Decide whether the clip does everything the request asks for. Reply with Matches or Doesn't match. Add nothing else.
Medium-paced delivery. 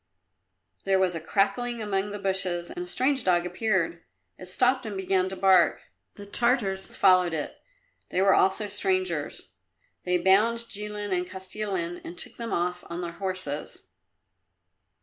Matches